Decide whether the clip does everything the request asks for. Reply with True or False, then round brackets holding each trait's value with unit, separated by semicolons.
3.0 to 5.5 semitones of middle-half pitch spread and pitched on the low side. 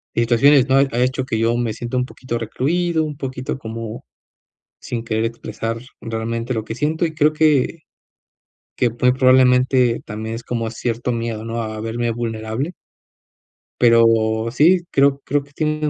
True (3.3 semitones; 120 Hz)